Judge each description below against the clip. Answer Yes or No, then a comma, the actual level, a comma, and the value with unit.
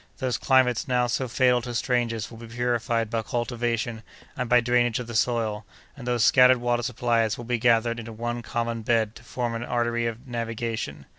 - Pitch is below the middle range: Yes, low, 120 Hz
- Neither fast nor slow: Yes, average, 195 wpm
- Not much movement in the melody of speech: Yes, narrow, 1.1 semitones